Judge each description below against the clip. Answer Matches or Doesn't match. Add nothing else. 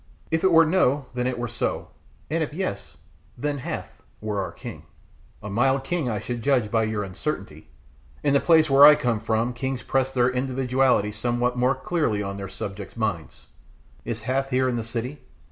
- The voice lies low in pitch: Matches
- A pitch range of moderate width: Matches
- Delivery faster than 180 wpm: Matches